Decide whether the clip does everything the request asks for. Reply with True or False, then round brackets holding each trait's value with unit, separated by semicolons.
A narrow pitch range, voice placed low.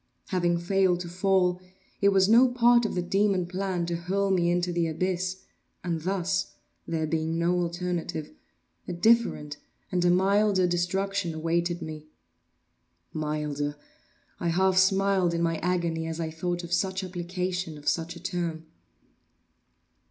False (2.1 semitones; 175 Hz)